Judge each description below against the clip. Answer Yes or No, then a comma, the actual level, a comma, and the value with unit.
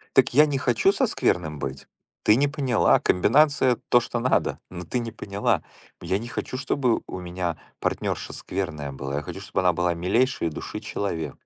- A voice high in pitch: No, low, 100 Hz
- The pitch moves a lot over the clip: Yes, wide, 6.9 semitones